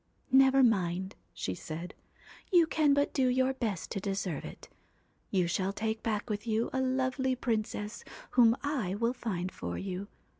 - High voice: Yes, high, 220 Hz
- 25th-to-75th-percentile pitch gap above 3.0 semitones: Yes, average, 5.3 semitones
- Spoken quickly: No, average, 175 wpm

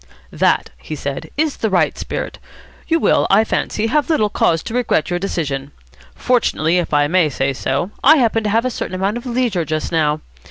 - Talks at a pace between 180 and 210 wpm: Yes, average, 200 wpm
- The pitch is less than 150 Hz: No, high, 190 Hz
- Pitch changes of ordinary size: No, wide, 7.3 semitones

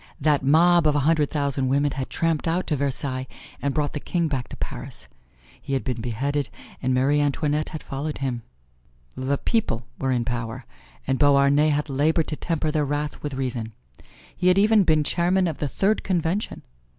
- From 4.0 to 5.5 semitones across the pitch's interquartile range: No, average, 3.1 semitones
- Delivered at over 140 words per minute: Yes, average, 185 wpm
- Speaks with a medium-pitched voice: Yes, medium, 145 Hz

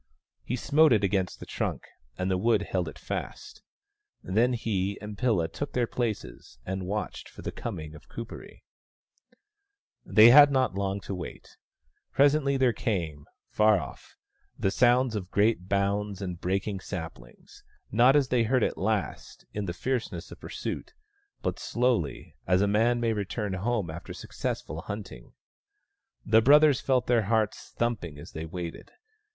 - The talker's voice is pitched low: Yes, low, 105 Hz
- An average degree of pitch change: Yes, average, 4.5 semitones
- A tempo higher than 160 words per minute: No, average, 155 wpm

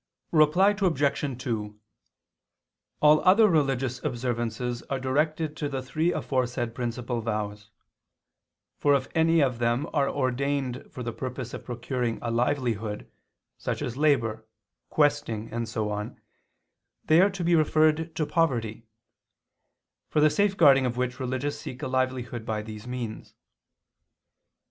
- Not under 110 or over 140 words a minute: Yes, slow, 135 wpm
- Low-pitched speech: Yes, low, 130 Hz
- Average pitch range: Yes, average, 4.2 semitones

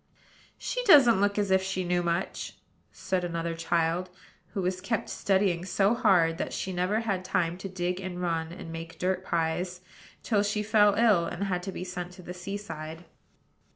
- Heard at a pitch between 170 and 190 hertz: Yes, medium, 185 Hz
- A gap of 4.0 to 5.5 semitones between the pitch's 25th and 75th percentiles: No, narrow, 2.5 semitones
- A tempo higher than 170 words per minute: Yes, average, 190 wpm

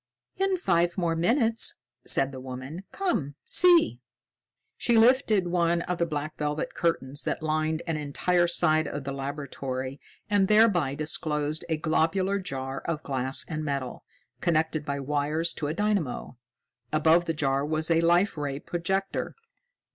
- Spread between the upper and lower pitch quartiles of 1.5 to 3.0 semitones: No, average, 3.6 semitones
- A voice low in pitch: No, medium, 160 Hz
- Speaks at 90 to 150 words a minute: Yes, average, 145 wpm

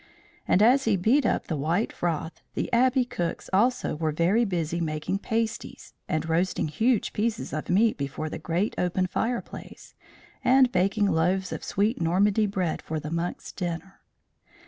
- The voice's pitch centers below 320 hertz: Yes, medium, 185 Hz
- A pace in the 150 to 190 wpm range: Yes, average, 160 wpm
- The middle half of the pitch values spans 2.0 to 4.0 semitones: No, average, 5.1 semitones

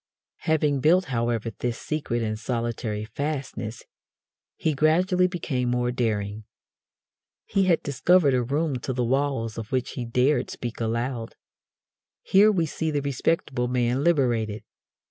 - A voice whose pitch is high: No, low, 125 Hz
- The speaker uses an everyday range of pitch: Yes, average, 4.6 semitones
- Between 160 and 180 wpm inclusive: No, slow, 135 wpm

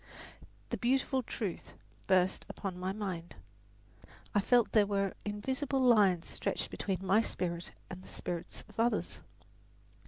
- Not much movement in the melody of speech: No, average, 4.0 semitones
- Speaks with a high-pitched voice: Yes, high, 200 Hz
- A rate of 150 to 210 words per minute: No, slow, 135 wpm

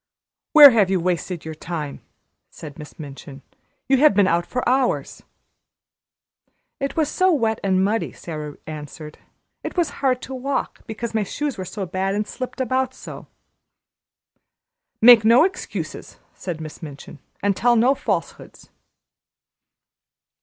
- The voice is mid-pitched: No, high, 210 Hz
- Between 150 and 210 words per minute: No, average, 140 wpm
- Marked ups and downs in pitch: Yes, wide, 7.5 semitones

